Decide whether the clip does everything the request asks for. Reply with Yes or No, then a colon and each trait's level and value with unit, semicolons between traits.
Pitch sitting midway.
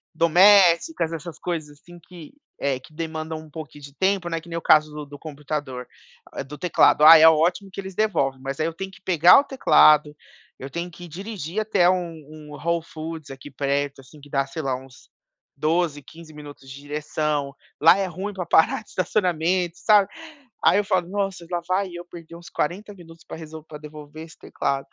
Yes: medium, 160 Hz